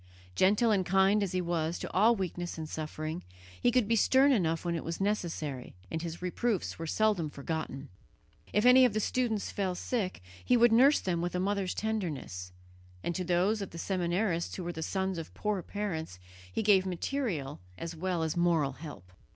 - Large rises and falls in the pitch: No, average, 4.2 semitones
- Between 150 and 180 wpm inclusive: No, average, 190 wpm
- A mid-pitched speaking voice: Yes, medium, 180 Hz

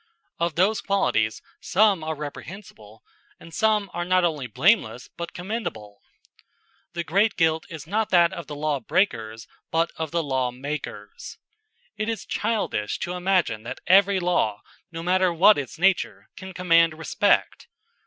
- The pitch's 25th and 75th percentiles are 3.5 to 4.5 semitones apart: No, average, 5.1 semitones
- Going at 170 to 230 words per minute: No, average, 150 wpm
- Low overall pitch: No, medium, 170 Hz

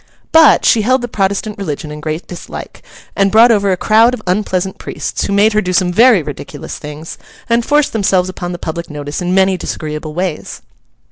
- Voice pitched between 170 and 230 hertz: Yes, high, 190 Hz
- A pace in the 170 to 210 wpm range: Yes, average, 195 wpm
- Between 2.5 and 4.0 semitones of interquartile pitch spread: No, average, 4.6 semitones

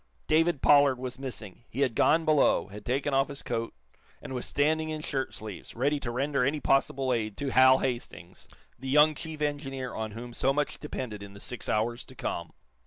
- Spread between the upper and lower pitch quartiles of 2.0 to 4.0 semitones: Yes, average, 3.5 semitones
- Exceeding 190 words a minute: Yes, average, 200 wpm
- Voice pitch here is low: Yes, low, 130 Hz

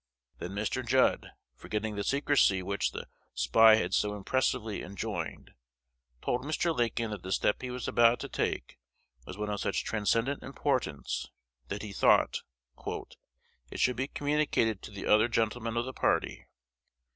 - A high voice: No, low, 110 Hz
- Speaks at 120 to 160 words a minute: Yes, average, 155 wpm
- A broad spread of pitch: No, average, 3.8 semitones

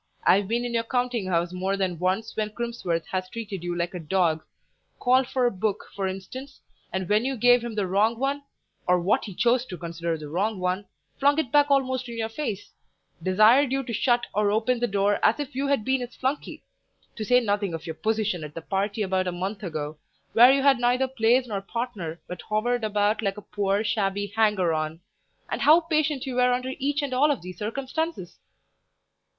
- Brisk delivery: Yes, fast, 210 wpm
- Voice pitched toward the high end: Yes, high, 215 Hz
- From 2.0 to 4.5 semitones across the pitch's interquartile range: No, average, 5.1 semitones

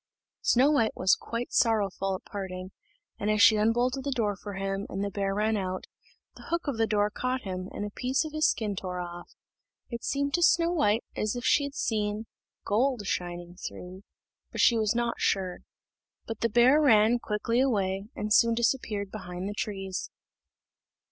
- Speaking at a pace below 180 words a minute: No, average, 185 wpm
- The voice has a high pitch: Yes, high, 215 Hz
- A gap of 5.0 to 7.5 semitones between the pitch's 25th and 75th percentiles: No, average, 3.7 semitones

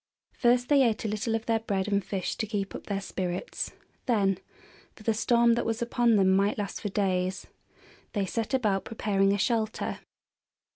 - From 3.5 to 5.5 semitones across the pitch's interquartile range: No, average, 2.8 semitones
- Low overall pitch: No, high, 210 Hz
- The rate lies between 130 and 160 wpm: No, average, 185 wpm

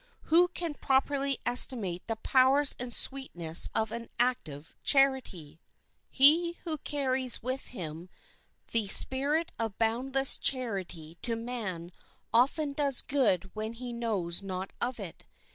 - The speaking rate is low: Yes, slow, 130 wpm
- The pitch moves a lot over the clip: Yes, wide, 5.8 semitones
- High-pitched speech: Yes, high, 245 Hz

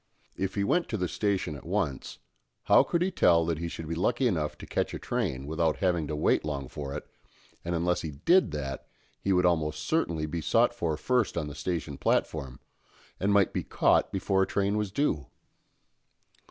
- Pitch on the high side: No, very low, 85 Hz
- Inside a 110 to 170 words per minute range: No, average, 200 wpm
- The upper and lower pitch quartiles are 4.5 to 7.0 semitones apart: Yes, average, 4.8 semitones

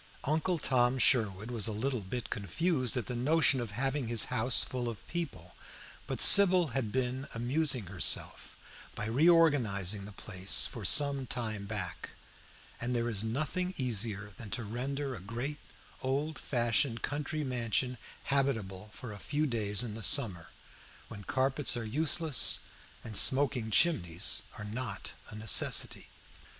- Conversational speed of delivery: Yes, average, 145 wpm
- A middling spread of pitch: Yes, average, 4.5 semitones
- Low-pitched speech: Yes, low, 120 Hz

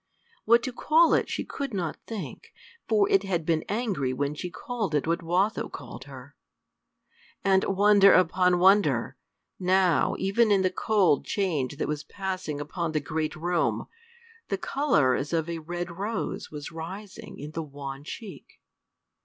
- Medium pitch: Yes, medium, 180 Hz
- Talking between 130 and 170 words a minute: Yes, average, 160 wpm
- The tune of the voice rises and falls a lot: No, average, 4.7 semitones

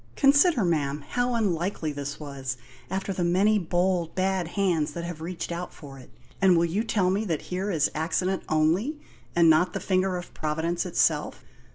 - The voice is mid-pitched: Yes, medium, 175 Hz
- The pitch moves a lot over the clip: No, average, 3.2 semitones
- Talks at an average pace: Yes, average, 180 wpm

